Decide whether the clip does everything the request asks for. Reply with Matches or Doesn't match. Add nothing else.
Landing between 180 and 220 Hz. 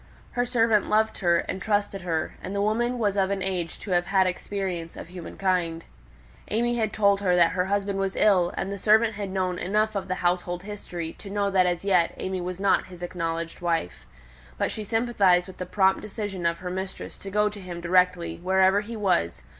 Matches